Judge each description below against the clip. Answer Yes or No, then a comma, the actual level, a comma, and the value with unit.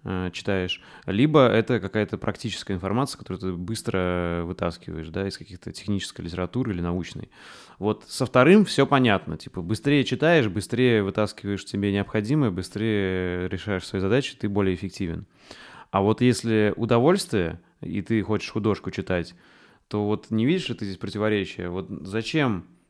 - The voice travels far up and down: No, average, 3.6 semitones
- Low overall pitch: Yes, low, 105 Hz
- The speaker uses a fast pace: No, average, 145 wpm